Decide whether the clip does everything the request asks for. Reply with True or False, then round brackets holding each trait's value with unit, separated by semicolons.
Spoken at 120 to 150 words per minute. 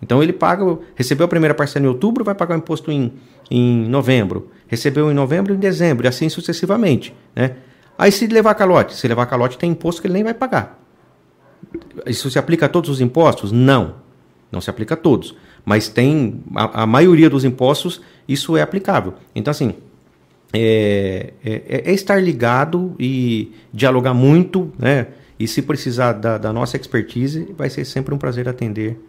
False (175 wpm)